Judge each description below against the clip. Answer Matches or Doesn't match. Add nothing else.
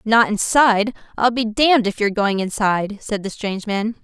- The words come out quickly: Doesn't match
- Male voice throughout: Doesn't match